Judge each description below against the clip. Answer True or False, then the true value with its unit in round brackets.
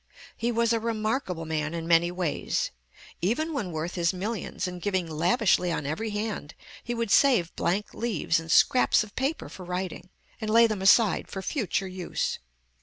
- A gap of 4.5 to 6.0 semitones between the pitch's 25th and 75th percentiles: True (4.9 semitones)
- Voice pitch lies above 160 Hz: True (190 Hz)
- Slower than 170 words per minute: False (175 wpm)